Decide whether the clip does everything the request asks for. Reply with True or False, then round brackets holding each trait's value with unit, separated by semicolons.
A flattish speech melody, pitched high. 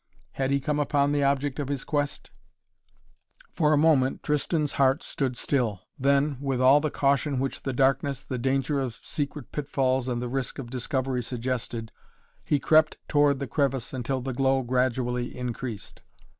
False (2.0 semitones; 135 Hz)